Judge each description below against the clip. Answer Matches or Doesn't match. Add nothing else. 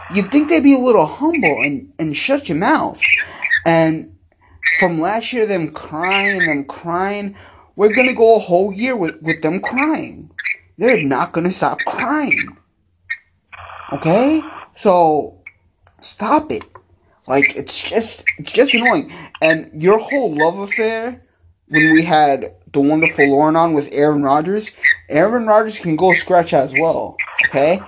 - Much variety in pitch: Matches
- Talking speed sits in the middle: Matches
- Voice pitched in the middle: Matches